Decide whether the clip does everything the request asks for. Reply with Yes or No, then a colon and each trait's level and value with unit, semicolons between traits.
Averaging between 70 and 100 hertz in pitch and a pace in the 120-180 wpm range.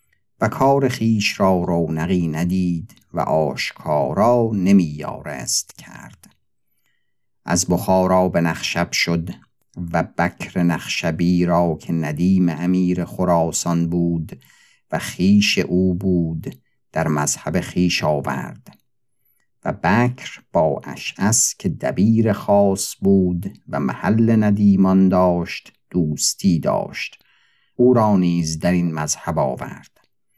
No: very low, 90 Hz; slow, 105 wpm